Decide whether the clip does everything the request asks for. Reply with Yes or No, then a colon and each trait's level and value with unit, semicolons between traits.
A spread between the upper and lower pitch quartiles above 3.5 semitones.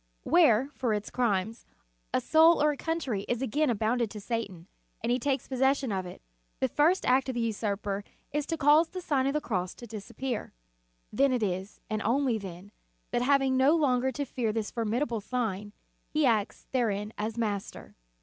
Yes: average, 4.7 semitones